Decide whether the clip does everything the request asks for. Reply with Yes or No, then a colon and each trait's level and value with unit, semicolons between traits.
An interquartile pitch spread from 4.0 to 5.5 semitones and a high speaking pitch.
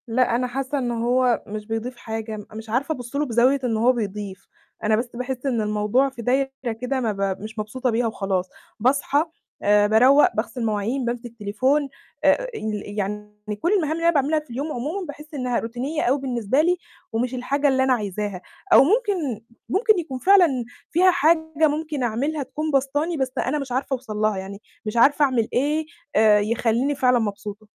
Yes: average, 4.6 semitones; very high, 250 Hz